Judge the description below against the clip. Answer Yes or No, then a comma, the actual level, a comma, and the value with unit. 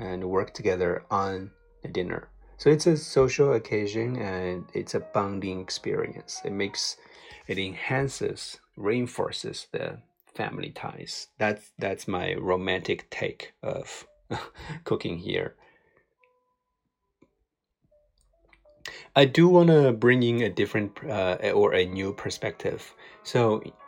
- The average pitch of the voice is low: Yes, low, 120 Hz